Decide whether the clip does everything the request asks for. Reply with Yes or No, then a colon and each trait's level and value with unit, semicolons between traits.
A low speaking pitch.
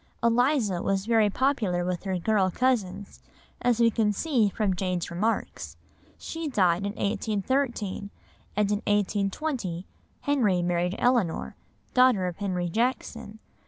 No: high, 205 Hz